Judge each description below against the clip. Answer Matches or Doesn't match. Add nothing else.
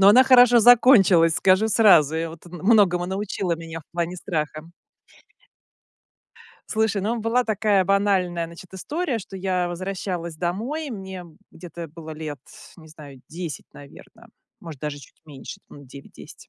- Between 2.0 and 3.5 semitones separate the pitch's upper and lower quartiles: Doesn't match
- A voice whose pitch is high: Doesn't match